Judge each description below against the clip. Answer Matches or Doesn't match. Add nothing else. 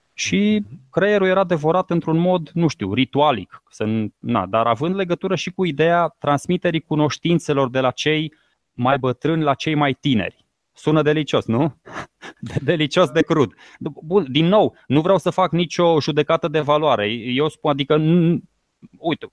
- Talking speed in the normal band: Matches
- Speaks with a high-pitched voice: Doesn't match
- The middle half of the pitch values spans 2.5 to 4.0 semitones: Matches